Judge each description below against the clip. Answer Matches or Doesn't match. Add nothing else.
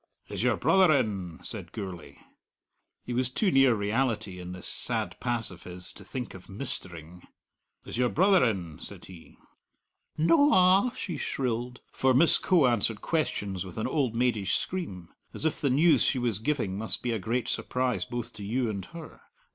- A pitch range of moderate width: Doesn't match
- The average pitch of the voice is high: Doesn't match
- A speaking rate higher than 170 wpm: Matches